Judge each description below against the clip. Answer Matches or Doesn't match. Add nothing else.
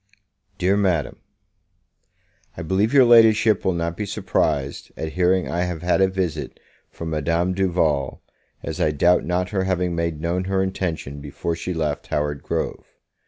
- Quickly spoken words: Doesn't match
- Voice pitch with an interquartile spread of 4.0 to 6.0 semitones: Doesn't match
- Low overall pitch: Matches